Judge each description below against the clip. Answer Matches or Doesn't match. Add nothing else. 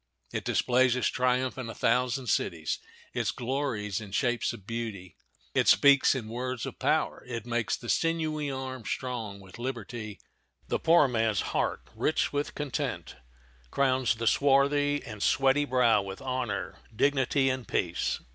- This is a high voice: Doesn't match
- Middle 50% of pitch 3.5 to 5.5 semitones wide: Doesn't match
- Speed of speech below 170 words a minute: Matches